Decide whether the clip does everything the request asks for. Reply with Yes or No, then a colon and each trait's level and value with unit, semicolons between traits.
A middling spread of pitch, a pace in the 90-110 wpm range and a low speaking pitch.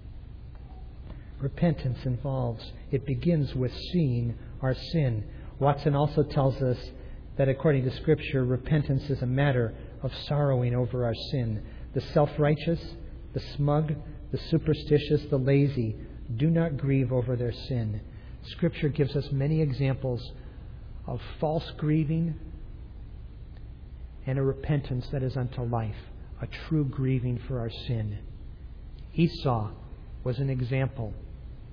No: average, 3.6 semitones; slow, 120 wpm; low, 130 Hz